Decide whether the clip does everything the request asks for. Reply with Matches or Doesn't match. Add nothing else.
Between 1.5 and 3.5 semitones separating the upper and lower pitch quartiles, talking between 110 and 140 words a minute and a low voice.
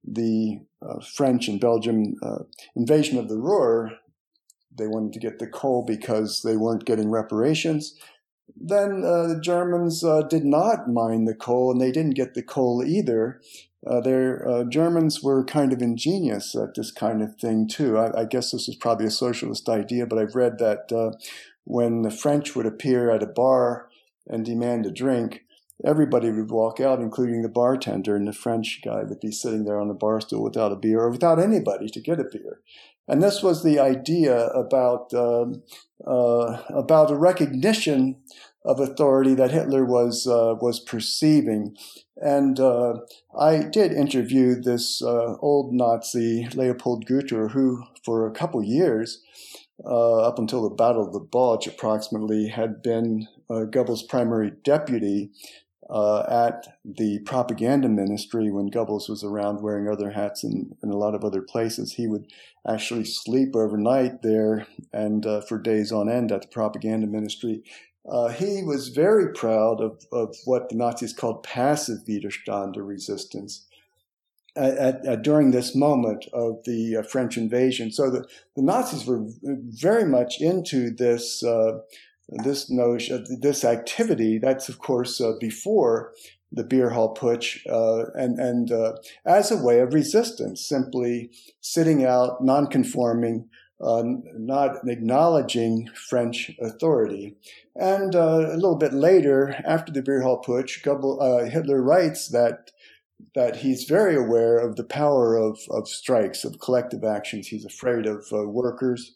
Doesn't match